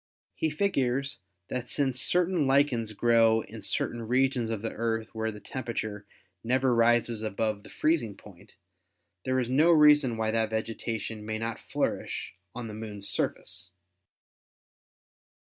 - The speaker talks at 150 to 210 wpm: No, average, 140 wpm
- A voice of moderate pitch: No, low, 115 Hz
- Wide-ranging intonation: No, average, 3.0 semitones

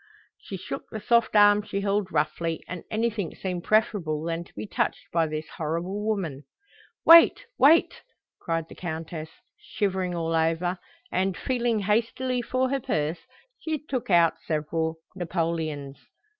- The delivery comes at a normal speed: Yes, average, 145 wpm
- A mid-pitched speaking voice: Yes, medium, 180 Hz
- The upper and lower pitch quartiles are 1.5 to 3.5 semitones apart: No, average, 4.9 semitones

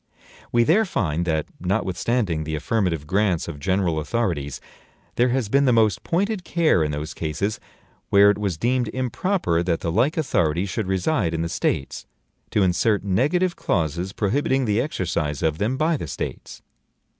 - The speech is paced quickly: No, average, 165 wpm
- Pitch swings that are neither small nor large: No, wide, 7.0 semitones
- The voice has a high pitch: No, low, 100 Hz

